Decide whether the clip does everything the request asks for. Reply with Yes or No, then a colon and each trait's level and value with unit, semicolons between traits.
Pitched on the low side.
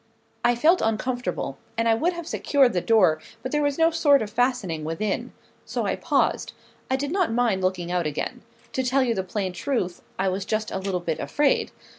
No: high, 225 Hz